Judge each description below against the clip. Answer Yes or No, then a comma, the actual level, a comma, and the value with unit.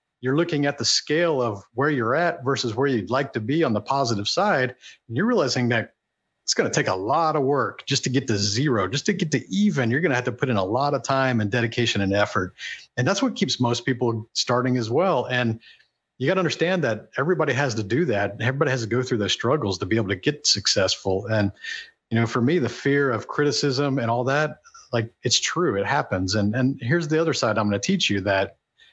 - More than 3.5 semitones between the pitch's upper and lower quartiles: Yes, average, 4.1 semitones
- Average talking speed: No, fast, 245 wpm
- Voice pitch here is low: Yes, low, 125 Hz